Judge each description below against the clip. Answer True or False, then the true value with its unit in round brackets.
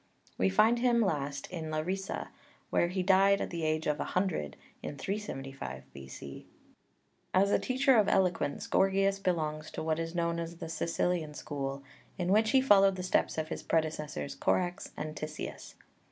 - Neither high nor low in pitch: True (170 Hz)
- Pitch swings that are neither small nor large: True (4.2 semitones)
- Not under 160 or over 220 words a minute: True (170 wpm)